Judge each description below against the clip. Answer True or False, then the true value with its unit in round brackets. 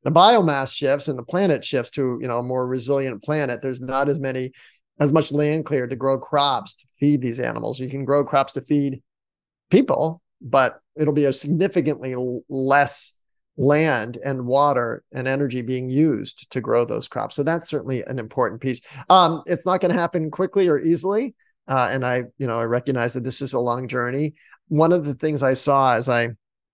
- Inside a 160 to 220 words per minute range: True (200 wpm)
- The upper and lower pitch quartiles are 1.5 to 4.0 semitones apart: True (3.1 semitones)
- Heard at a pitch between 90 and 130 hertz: False (140 Hz)